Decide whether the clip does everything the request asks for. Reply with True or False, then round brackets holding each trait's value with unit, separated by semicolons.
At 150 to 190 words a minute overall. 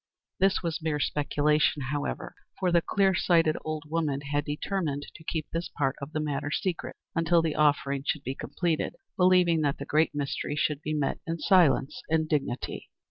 True (180 wpm)